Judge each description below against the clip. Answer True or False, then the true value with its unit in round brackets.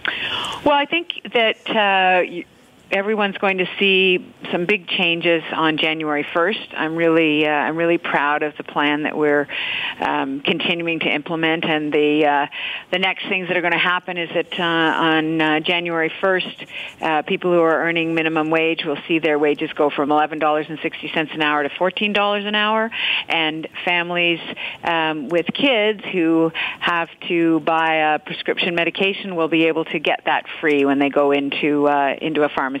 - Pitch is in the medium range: True (165 Hz)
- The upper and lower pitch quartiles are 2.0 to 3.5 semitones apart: True (3.0 semitones)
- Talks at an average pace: True (175 wpm)